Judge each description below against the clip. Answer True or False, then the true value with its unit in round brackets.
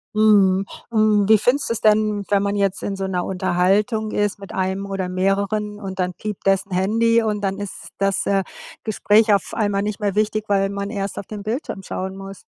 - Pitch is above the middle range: True (200 Hz)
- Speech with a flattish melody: True (1.6 semitones)